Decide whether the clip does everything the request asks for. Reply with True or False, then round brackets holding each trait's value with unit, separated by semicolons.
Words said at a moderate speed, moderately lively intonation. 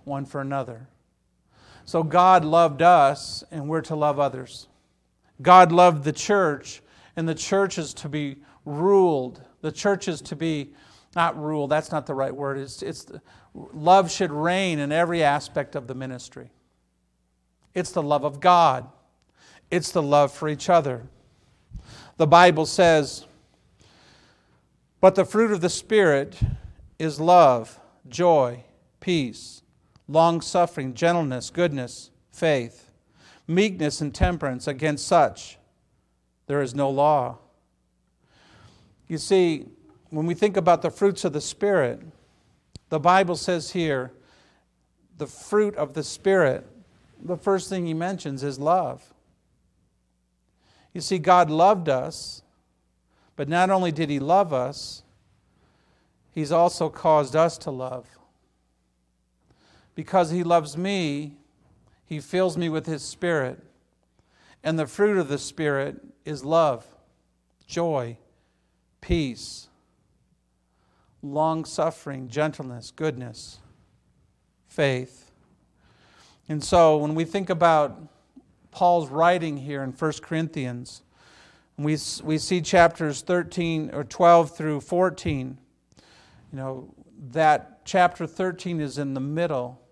False (120 wpm; 4.9 semitones)